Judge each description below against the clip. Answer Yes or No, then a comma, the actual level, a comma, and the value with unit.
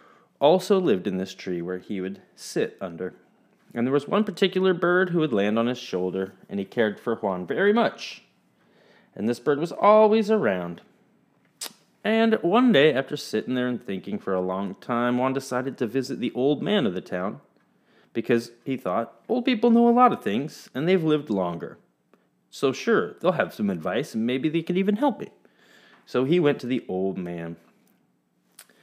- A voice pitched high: No, low, 125 Hz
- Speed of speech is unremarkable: Yes, average, 190 wpm